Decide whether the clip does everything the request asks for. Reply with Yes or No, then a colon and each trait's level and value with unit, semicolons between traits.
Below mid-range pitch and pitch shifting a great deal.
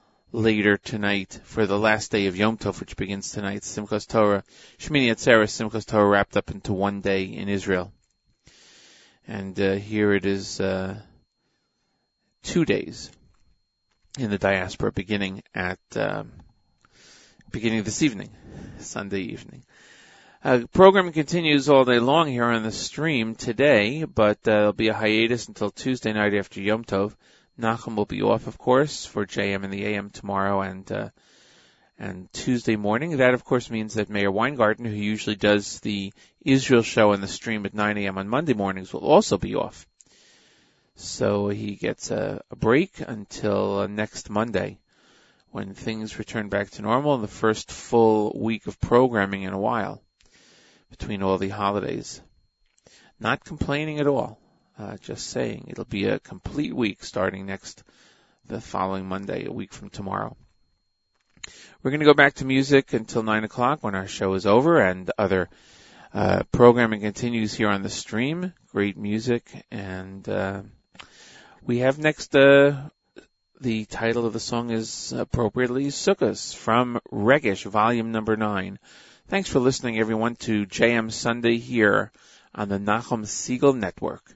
No: low, 110 Hz; average, 3.2 semitones